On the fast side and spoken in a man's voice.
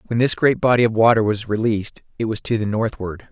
Yes: fast, 235 wpm; male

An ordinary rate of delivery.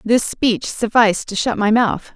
Yes: average, 195 wpm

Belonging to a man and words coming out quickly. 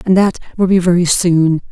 No: female; fast, 210 wpm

